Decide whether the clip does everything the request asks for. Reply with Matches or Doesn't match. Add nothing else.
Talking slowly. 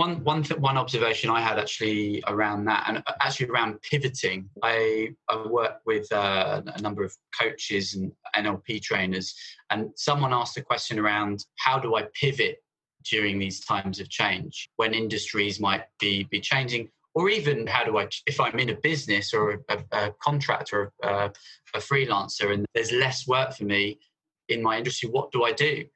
Doesn't match